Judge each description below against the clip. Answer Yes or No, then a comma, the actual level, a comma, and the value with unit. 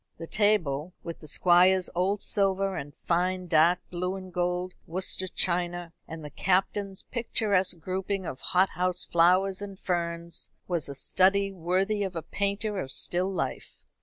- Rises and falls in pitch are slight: Yes, narrow, 2.1 semitones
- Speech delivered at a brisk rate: No, average, 150 wpm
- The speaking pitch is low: No, medium, 185 Hz